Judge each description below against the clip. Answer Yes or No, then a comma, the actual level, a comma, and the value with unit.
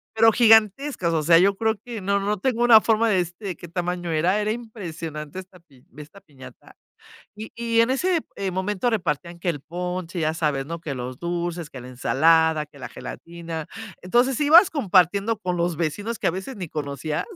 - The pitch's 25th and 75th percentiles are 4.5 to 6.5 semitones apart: Yes, average, 5.1 semitones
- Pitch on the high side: No, medium, 180 Hz